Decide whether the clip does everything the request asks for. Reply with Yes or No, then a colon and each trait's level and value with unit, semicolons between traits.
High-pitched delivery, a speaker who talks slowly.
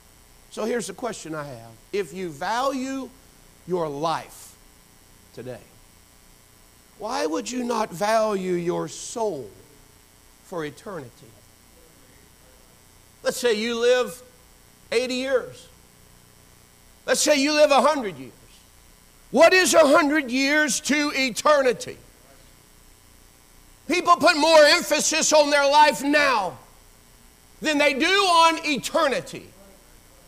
Yes: high, 235 Hz; slow, 105 wpm